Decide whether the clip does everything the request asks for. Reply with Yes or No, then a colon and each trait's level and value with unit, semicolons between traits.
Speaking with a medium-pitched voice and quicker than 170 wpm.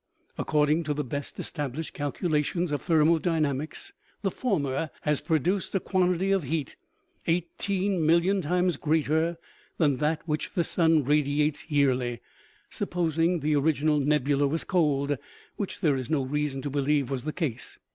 No: medium, 155 Hz; average, 150 wpm